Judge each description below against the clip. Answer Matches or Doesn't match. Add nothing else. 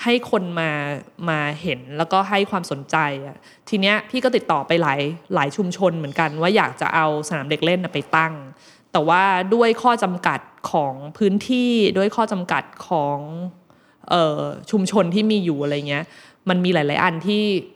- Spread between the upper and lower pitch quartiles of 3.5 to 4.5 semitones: Doesn't match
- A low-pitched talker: Doesn't match